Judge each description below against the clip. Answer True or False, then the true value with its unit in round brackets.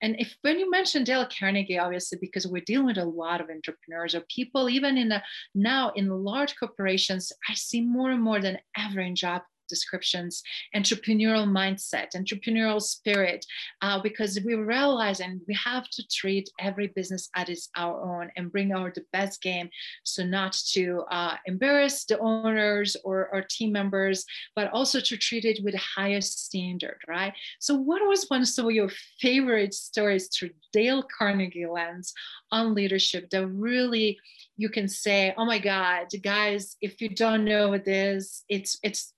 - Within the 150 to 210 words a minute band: True (170 wpm)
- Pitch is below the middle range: False (200 Hz)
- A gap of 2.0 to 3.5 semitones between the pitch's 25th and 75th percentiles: True (3.1 semitones)